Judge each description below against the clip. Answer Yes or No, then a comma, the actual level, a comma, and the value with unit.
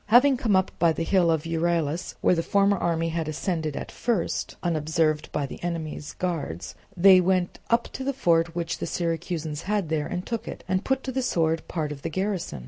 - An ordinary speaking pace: No, fast, 210 wpm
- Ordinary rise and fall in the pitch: Yes, average, 3.0 semitones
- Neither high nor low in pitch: Yes, medium, 170 Hz